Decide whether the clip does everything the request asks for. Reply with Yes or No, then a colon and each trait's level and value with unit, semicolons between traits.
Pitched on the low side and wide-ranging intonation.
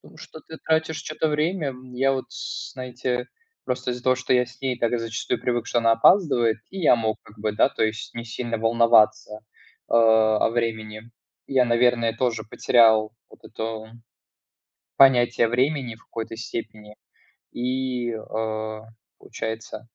No: low, 120 Hz; narrow, 2.4 semitones